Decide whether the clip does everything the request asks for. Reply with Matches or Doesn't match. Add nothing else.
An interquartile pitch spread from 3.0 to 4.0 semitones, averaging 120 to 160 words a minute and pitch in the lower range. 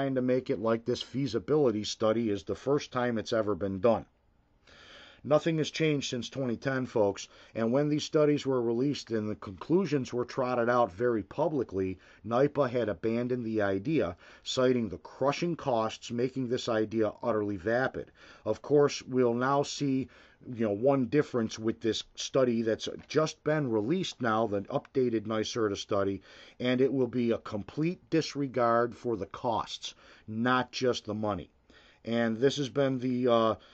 Matches